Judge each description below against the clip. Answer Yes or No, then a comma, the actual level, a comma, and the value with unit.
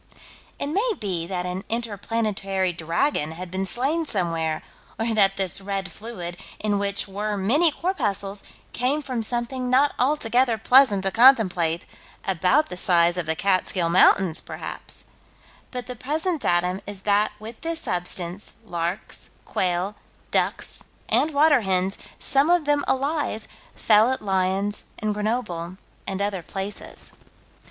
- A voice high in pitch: Yes, high, 205 Hz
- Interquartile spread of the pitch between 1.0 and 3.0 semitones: No, average, 5.3 semitones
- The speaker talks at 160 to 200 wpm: No, average, 140 wpm